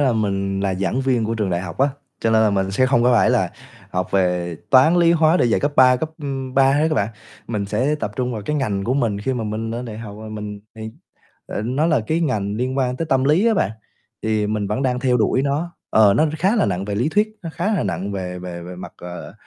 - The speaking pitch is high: No, low, 115 Hz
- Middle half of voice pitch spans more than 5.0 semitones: Yes, wide, 5.4 semitones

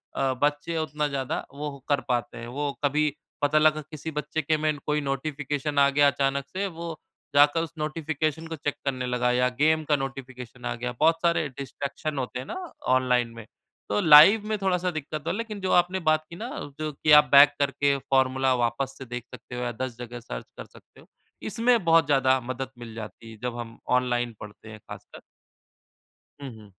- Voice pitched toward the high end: No, medium, 140 Hz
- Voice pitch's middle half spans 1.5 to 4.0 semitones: Yes, average, 3.6 semitones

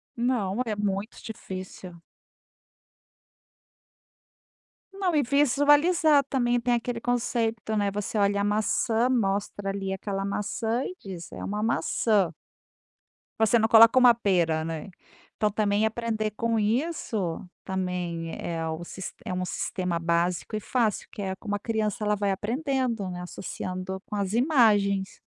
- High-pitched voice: Yes, high, 210 Hz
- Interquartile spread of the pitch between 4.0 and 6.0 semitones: No, average, 3.6 semitones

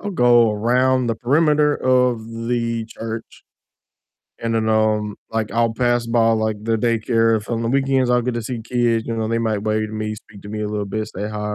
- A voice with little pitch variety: Yes, narrow, 1.9 semitones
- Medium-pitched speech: No, low, 115 Hz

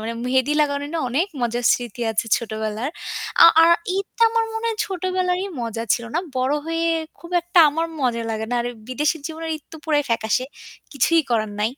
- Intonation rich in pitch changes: Yes, wide, 6.2 semitones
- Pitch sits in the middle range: No, very high, 285 Hz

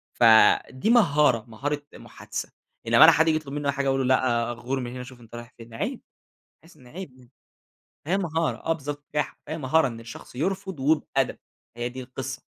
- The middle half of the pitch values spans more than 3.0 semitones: Yes, average, 4.3 semitones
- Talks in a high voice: No, low, 135 Hz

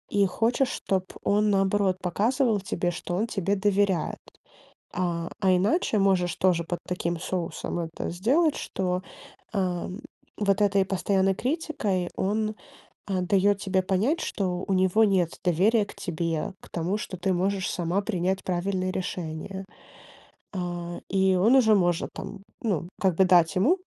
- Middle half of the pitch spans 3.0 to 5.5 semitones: No, narrow, 2.4 semitones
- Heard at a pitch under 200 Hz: Yes, high, 190 Hz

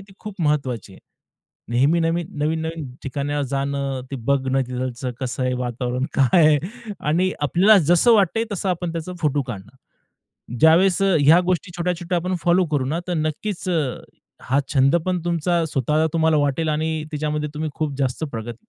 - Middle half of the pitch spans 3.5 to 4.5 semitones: Yes, average, 4.2 semitones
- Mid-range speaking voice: Yes, medium, 155 Hz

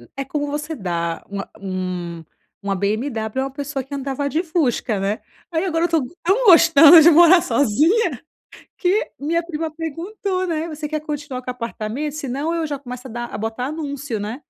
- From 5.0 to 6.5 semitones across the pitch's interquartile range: Yes, wide, 5.5 semitones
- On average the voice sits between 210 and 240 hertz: No, very high, 285 Hz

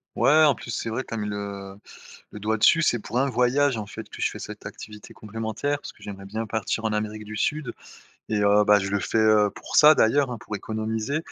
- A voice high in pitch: No, low, 110 Hz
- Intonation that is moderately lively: Yes, average, 3.1 semitones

